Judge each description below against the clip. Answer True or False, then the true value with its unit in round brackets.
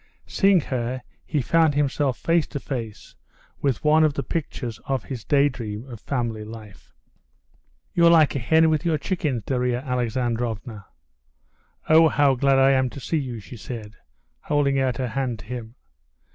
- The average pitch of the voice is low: True (130 Hz)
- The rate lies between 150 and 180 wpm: True (160 wpm)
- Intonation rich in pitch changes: False (3.8 semitones)